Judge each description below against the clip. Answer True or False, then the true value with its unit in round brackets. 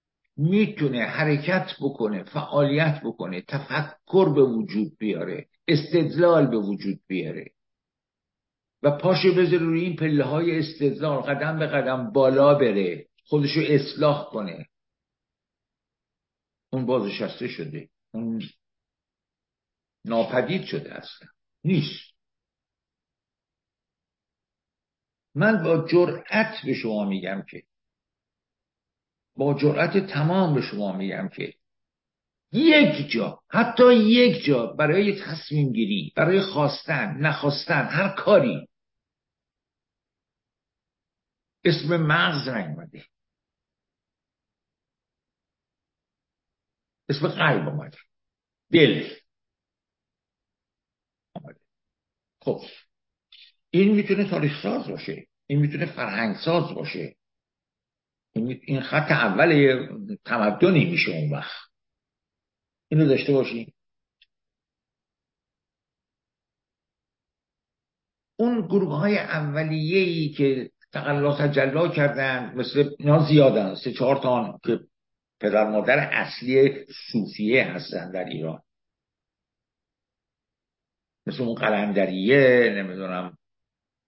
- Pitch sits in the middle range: True (145 Hz)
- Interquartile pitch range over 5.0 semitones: True (5.4 semitones)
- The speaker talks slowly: True (85 wpm)